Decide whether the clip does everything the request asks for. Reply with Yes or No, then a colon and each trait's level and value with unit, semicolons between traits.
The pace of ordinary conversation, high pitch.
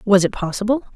Yes: average, 190 wpm; high, 210 Hz